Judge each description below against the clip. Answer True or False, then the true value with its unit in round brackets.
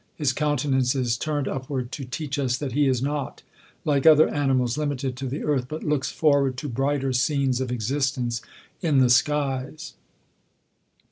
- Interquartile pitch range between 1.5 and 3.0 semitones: True (2.4 semitones)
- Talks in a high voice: False (135 Hz)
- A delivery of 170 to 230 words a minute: False (160 wpm)